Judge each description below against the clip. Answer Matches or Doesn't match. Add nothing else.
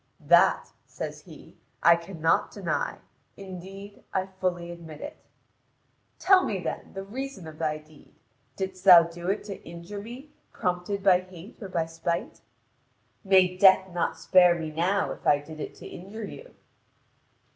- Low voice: Doesn't match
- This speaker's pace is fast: Doesn't match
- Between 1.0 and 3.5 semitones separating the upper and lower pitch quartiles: Matches